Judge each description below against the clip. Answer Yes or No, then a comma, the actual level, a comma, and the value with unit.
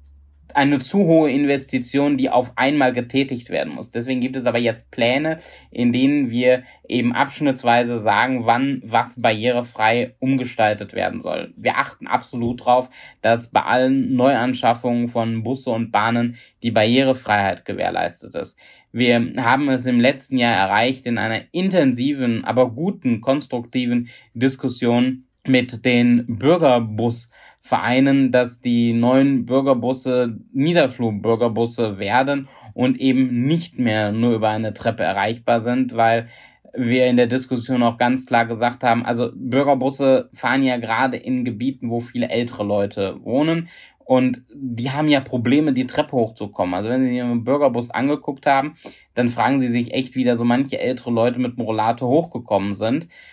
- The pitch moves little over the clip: Yes, narrow, 2.0 semitones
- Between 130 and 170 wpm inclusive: Yes, average, 145 wpm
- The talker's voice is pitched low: Yes, low, 125 Hz